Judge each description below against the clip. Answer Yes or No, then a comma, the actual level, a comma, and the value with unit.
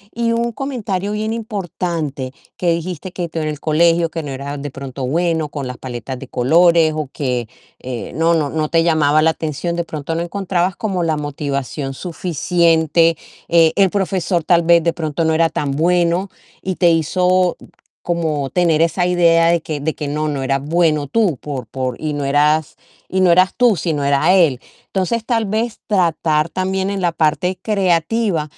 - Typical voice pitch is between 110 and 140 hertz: No, medium, 165 Hz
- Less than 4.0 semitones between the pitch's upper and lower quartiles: Yes, average, 3.4 semitones